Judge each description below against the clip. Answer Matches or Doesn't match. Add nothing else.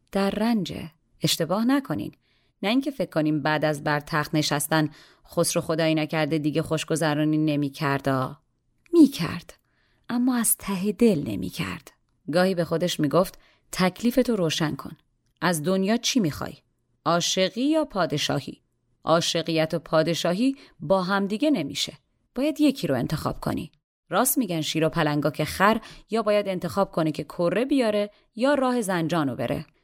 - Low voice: Doesn't match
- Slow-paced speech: Doesn't match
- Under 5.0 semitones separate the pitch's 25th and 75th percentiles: Doesn't match